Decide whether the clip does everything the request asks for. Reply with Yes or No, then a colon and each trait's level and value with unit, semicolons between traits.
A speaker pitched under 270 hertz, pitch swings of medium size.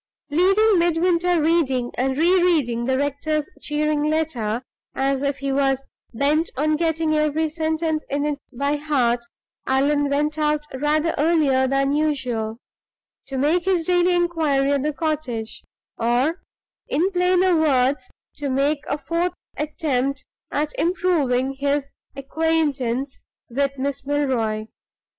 No: very high, 290 Hz; average, 3.0 semitones